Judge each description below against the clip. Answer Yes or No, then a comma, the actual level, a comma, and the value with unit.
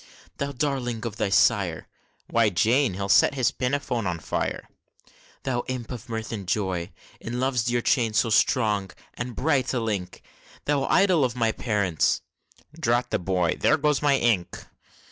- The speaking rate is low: No, average, 165 wpm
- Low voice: Yes, low, 120 Hz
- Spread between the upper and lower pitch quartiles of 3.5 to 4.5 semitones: Yes, average, 4.0 semitones